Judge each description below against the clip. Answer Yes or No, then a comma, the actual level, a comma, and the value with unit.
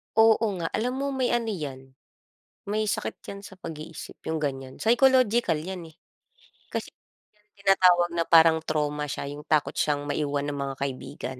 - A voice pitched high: No, medium, 165 Hz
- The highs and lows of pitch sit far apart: Yes, wide, 6.3 semitones